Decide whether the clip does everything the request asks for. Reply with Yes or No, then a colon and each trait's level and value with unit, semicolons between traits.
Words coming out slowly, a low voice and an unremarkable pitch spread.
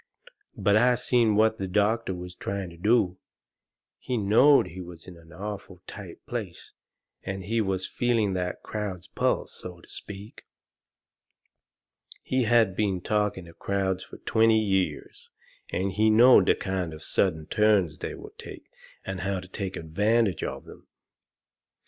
No: average, 155 wpm; low, 100 Hz; average, 3.0 semitones